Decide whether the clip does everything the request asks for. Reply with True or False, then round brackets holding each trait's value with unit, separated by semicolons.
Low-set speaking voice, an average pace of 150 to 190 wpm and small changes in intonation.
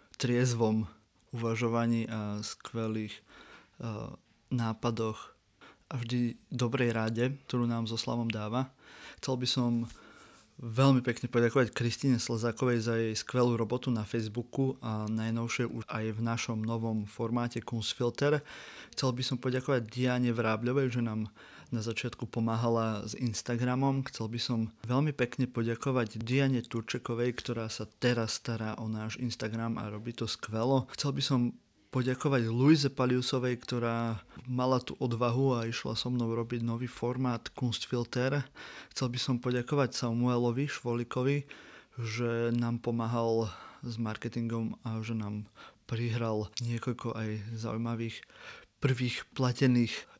False (120 Hz; 130 wpm; 1.7 semitones)